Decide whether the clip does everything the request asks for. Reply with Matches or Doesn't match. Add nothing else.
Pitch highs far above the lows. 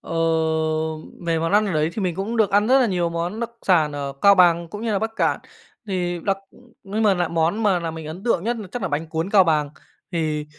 Doesn't match